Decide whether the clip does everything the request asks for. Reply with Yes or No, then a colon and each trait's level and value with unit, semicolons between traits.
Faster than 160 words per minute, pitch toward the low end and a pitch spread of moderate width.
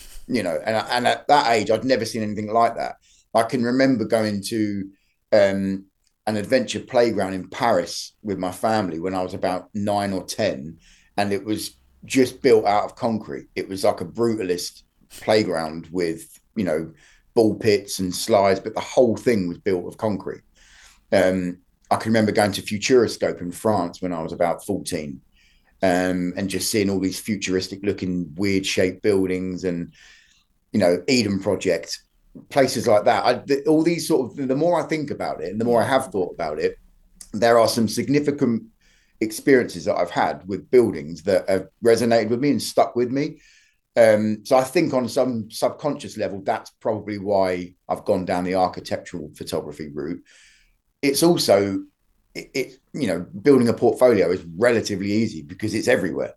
Yes: average, 175 wpm; low, 105 Hz; average, 4.2 semitones